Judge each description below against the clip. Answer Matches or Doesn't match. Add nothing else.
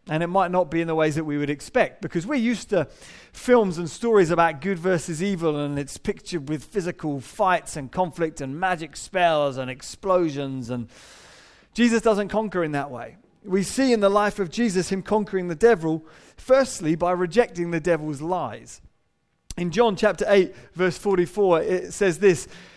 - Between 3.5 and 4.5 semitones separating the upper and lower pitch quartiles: Matches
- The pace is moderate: Matches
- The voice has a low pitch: Doesn't match